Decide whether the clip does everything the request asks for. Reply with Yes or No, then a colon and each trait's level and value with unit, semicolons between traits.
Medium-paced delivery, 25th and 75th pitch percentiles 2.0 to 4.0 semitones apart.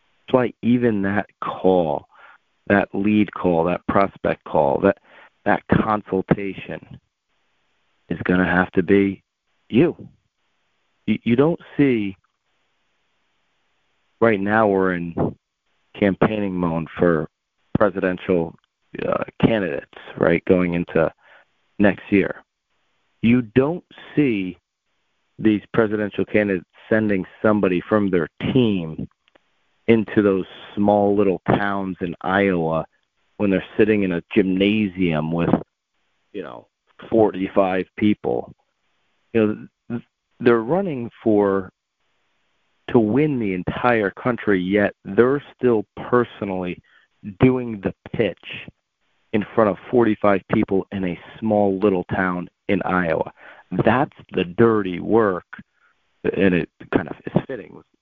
No: slow, 115 wpm; average, 3.1 semitones